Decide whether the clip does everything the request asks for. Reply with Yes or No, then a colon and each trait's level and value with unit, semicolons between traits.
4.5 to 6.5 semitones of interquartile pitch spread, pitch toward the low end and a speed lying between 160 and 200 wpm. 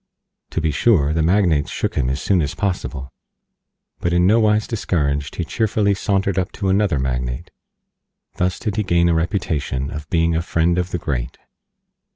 Yes: average, 5.2 semitones; very low, 85 Hz; average, 180 wpm